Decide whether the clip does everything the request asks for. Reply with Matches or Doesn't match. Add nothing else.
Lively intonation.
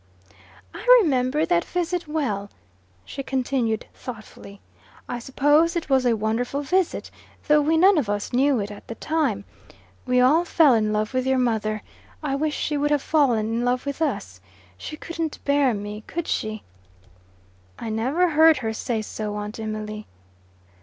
Matches